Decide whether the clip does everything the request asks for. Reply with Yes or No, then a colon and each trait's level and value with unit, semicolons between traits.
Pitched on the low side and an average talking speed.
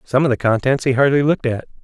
No: low, 130 Hz; fast, 260 wpm